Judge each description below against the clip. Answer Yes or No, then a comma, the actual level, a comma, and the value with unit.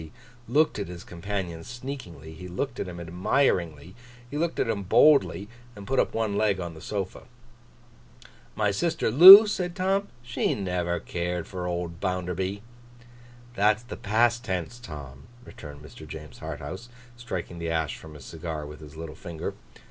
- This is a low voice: Yes, very low, 90 Hz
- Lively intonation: Yes, wide, 6.0 semitones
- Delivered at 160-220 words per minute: Yes, average, 165 wpm